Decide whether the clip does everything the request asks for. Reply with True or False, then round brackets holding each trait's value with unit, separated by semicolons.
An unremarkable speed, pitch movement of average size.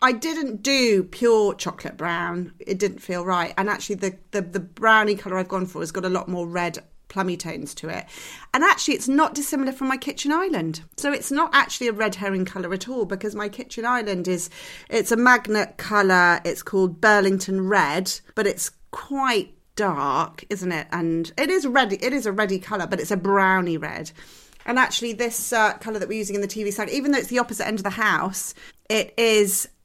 False (210 wpm; 4.4 semitones)